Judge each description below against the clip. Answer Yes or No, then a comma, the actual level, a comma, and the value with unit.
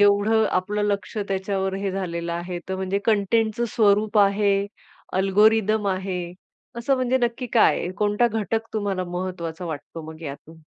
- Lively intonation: No, average, 2.7 semitones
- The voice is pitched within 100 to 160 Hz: No, high, 200 Hz